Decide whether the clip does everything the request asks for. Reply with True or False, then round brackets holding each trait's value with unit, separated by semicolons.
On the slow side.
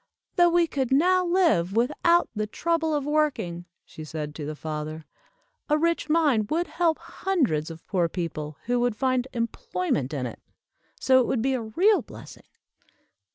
False (165 wpm)